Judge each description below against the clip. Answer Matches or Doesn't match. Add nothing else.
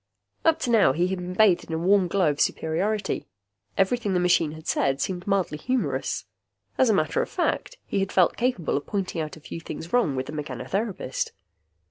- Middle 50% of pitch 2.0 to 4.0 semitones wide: Doesn't match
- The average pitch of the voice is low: Doesn't match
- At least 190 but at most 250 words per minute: Matches